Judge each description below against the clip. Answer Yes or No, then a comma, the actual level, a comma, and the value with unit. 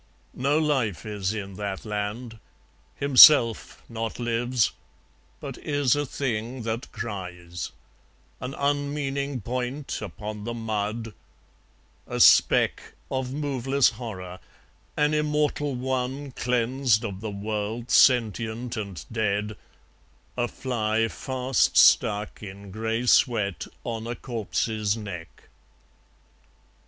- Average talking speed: No, slow, 105 wpm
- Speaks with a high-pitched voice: No, low, 115 Hz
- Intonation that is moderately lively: Yes, average, 3.7 semitones